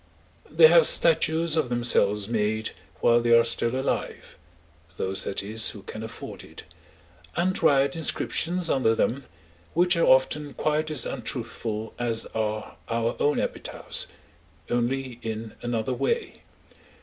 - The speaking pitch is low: Yes, low, 120 Hz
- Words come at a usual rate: No, slow, 130 wpm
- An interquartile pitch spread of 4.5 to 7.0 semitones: Yes, average, 5.1 semitones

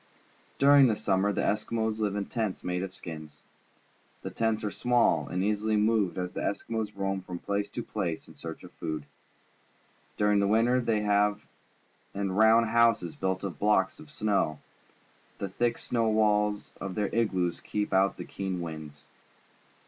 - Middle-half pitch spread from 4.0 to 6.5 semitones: No, average, 2.7 semitones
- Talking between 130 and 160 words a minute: No, average, 170 wpm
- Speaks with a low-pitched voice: Yes, low, 105 Hz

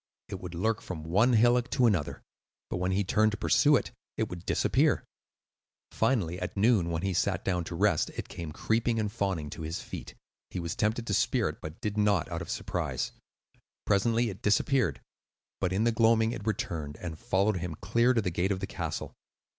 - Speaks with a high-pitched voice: No, low, 100 Hz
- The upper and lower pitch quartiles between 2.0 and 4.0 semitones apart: No, average, 4.4 semitones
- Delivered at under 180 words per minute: No, average, 200 wpm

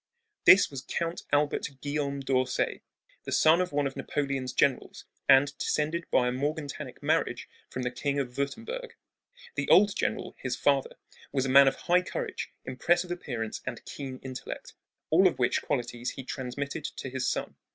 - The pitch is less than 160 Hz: Yes, medium, 140 Hz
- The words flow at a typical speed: Yes, average, 165 wpm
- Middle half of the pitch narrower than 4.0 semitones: Yes, average, 2.8 semitones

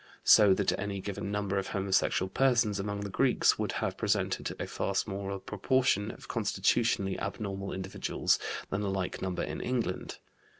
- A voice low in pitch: Yes, low, 100 Hz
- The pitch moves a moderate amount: No, narrow, 1.3 semitones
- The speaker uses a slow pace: No, average, 160 wpm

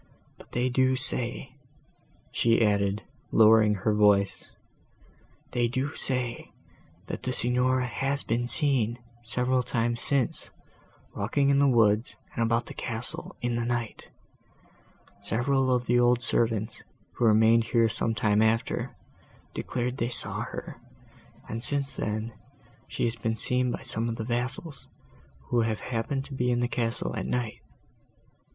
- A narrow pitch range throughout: Yes, narrow, 2.1 semitones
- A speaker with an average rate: Yes, average, 145 wpm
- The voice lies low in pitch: Yes, low, 120 Hz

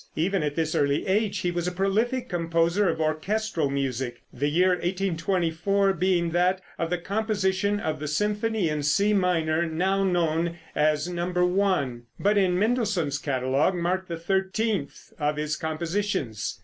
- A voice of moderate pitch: Yes, medium, 175 Hz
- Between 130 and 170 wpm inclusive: Yes, average, 150 wpm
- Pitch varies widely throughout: No, average, 3.9 semitones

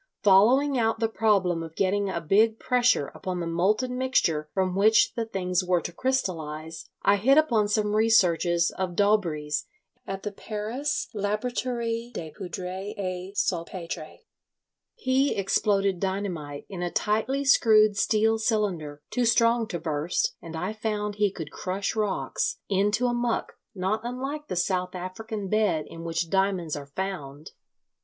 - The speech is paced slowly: No, average, 150 wpm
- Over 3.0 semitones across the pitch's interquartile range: Yes, average, 4.1 semitones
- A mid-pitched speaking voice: No, high, 200 Hz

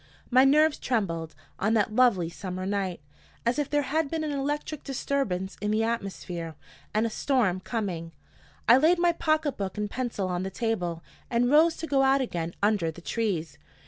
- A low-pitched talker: No, high, 225 Hz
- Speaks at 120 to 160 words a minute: No, average, 180 wpm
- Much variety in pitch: Yes, wide, 6.9 semitones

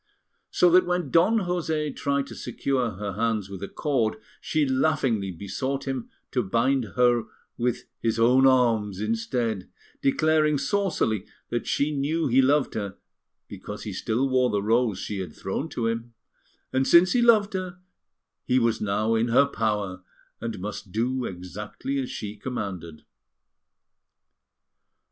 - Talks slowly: No, average, 150 wpm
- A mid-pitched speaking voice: No, low, 120 Hz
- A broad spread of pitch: No, average, 4.8 semitones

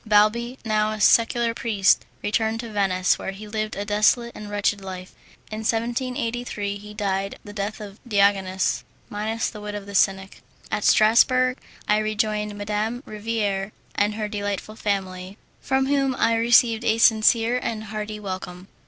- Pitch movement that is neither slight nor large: No, narrow, 2.0 semitones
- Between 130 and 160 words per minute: Yes, average, 155 wpm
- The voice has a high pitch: Yes, high, 210 Hz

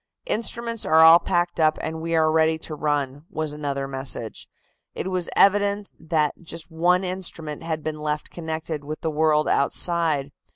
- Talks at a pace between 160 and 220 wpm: Yes, average, 165 wpm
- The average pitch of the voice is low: No, medium, 160 Hz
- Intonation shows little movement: Yes, narrow, 2.3 semitones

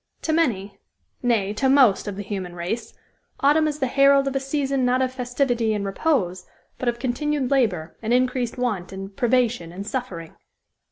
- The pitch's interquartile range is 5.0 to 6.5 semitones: Yes, average, 5.3 semitones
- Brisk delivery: No, average, 175 wpm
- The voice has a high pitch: Yes, high, 245 Hz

